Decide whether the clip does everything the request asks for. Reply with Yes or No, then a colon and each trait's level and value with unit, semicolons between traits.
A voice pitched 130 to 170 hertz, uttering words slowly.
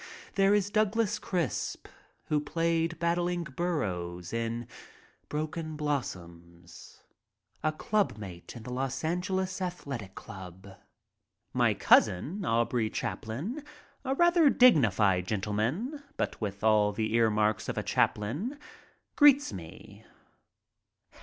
Yes: medium, 140 Hz; slow, 105 wpm